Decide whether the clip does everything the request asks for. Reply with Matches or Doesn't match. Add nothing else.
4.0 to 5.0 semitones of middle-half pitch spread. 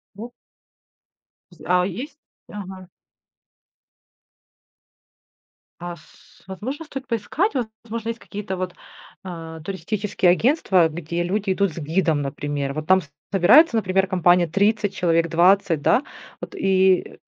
Doesn't match